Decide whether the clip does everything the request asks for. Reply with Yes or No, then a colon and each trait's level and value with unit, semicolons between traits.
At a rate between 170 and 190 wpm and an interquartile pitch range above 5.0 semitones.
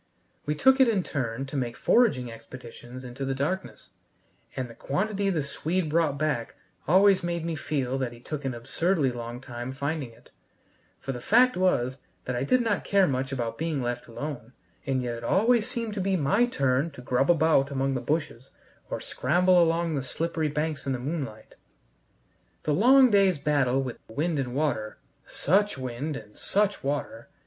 Yes: average, 180 wpm; wide, 5.5 semitones